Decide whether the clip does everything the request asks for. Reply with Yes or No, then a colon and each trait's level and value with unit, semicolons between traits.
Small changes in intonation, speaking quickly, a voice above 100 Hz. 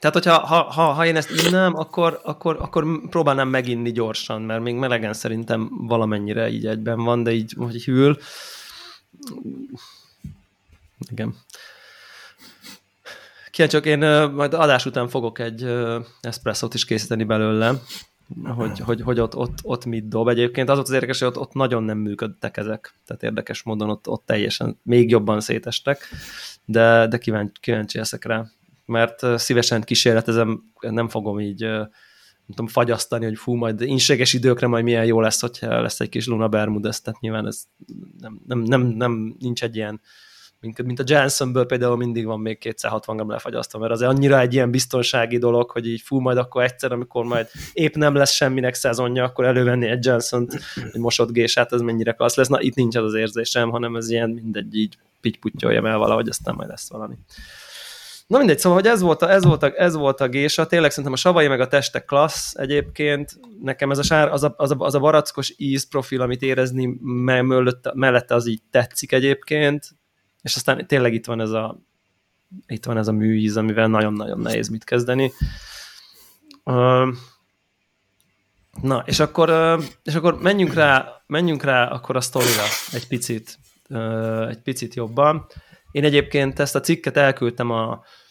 No: average, 3.5 semitones; fast, 170 wpm; low, 120 Hz